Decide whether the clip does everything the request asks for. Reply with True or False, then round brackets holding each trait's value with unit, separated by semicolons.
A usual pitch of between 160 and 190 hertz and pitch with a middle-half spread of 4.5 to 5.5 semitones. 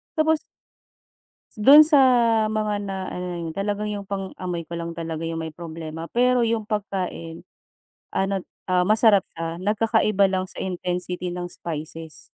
False (185 Hz; 4.0 semitones)